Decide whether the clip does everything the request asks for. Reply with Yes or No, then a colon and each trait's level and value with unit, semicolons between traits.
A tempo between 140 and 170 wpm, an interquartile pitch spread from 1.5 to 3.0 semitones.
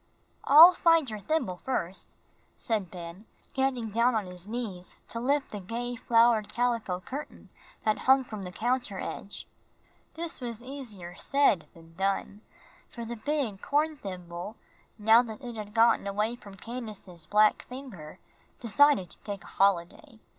No: average, 150 wpm; average, 4.5 semitones